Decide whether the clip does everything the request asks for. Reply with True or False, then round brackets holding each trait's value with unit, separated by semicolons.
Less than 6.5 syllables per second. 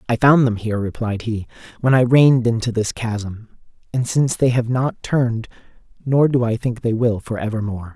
True (5.4 syllables/s)